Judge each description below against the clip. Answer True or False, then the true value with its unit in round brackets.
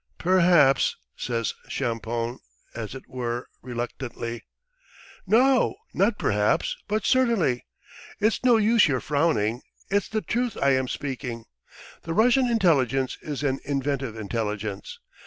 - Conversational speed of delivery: False (120 wpm)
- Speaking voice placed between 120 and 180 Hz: True (135 Hz)